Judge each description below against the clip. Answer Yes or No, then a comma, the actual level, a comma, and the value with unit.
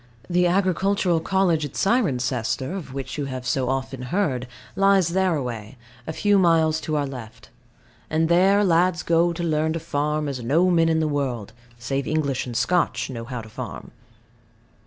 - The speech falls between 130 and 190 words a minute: Yes, average, 170 wpm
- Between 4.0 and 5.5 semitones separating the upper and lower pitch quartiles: Yes, average, 5.1 semitones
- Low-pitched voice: No, medium, 155 Hz